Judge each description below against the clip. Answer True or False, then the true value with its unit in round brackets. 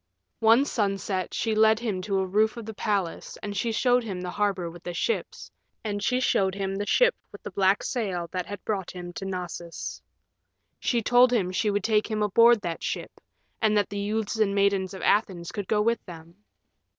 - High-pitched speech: True (205 Hz)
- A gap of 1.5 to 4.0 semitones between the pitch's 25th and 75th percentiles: True (2.8 semitones)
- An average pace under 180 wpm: False (205 wpm)